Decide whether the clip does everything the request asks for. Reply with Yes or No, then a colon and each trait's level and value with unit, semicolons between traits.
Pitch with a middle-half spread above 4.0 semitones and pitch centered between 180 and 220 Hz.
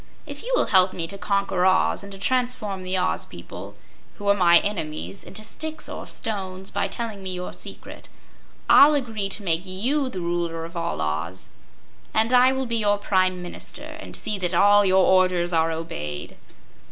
No: average, 3.7 semitones; high, 190 Hz